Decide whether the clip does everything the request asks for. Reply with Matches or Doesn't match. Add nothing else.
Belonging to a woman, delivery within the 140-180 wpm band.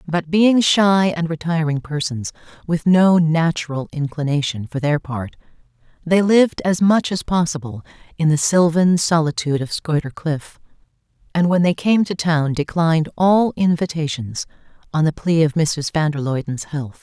Matches